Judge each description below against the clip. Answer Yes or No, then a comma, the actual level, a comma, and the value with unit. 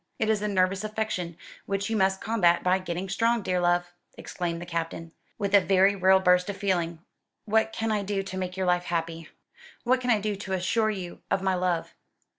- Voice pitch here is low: No, high, 190 Hz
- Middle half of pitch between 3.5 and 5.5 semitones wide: No, average, 2.7 semitones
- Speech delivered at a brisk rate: Yes, fast, 210 wpm